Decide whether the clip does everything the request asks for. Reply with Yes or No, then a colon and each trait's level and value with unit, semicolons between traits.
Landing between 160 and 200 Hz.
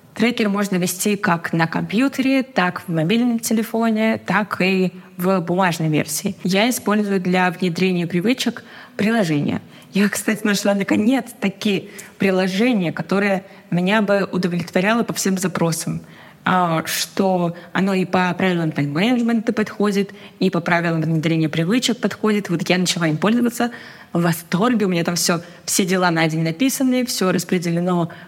Yes: high, 190 Hz